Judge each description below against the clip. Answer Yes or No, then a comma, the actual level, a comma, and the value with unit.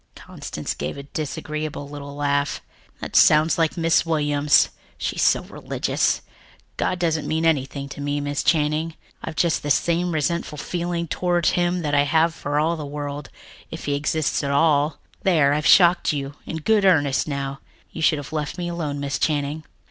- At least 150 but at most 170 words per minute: No, average, 180 wpm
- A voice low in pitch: No, medium, 150 Hz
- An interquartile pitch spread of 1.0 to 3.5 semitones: Yes, narrow, 2.4 semitones